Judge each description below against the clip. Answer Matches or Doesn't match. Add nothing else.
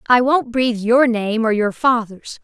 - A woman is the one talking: Matches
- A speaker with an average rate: Matches